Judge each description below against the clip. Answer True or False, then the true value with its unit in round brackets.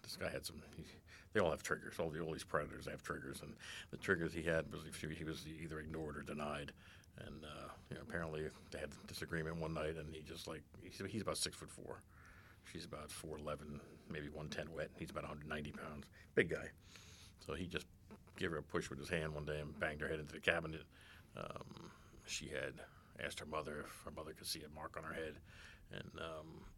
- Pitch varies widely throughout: False (2.8 semitones)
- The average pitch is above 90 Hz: False (80 Hz)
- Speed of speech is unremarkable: False (220 wpm)